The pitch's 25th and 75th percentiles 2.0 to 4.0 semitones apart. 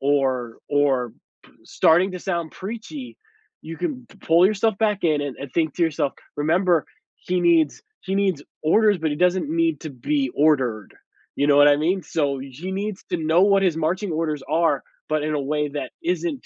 No: average, 4.8 semitones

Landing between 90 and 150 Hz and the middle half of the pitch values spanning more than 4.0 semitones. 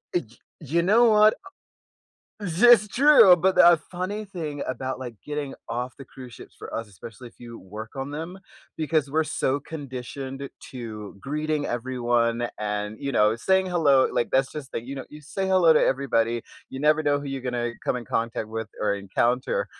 Yes: low, 135 Hz; average, 5.1 semitones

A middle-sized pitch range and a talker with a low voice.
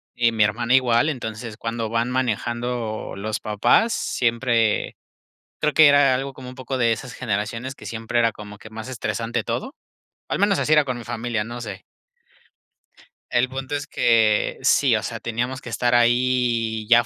No: narrow, 2.3 semitones; low, 120 Hz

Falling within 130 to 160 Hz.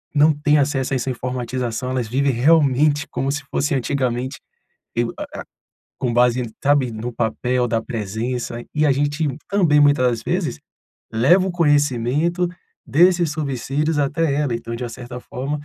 Yes: low, 135 Hz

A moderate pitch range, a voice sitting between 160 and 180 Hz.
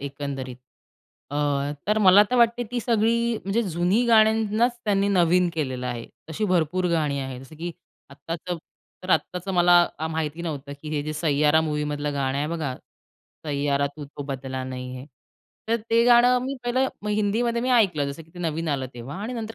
No: wide, 7.2 semitones; medium, 165 Hz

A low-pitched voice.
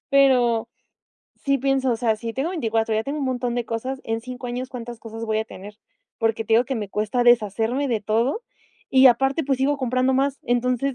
No: high, 245 Hz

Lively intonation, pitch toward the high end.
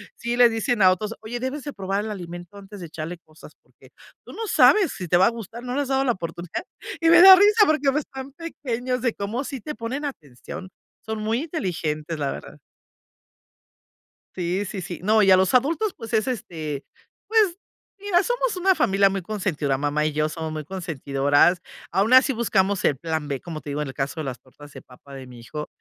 Yes: wide, 8.5 semitones; high, 200 Hz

